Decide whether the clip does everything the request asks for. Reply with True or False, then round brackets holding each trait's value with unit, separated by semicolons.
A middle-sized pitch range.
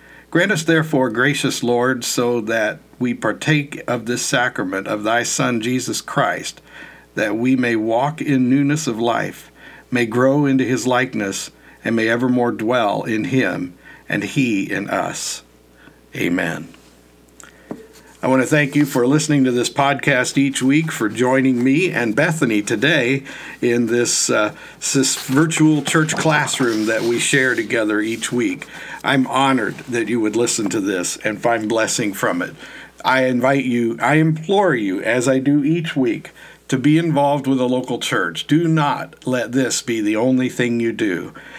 True (3.3 semitones)